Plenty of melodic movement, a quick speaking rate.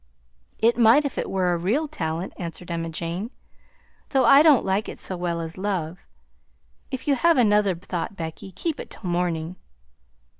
No: wide, 5.9 semitones; average, 175 wpm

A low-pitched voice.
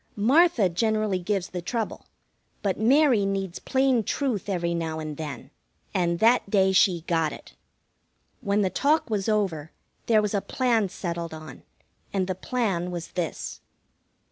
No: high, 195 Hz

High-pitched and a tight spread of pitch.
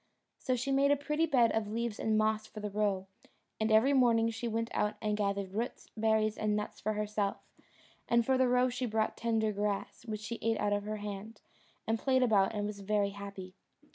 Yes: high, 215 Hz; narrow, 2.1 semitones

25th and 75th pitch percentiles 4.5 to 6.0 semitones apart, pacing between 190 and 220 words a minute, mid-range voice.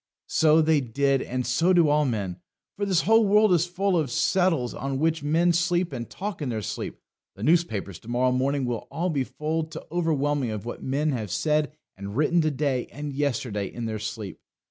Yes: average, 5.3 semitones; fast, 205 wpm; medium, 145 Hz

